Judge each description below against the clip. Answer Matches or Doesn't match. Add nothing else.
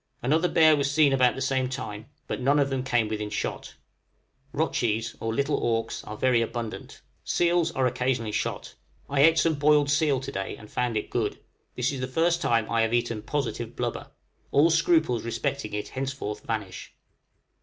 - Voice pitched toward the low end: Matches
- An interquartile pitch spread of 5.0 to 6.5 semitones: Doesn't match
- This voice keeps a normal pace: Matches